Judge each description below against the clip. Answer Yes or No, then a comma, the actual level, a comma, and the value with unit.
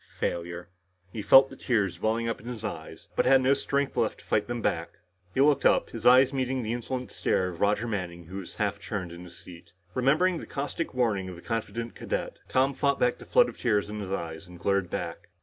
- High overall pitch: No, low, 110 Hz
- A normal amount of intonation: No, wide, 6.0 semitones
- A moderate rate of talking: No, fast, 220 wpm